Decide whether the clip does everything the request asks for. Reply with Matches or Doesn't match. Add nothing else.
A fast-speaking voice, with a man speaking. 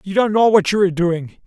Matches